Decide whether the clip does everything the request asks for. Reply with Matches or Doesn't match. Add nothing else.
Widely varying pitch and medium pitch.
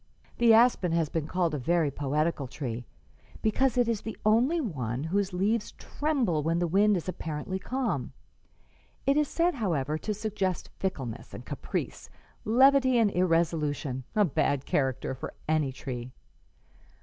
Matches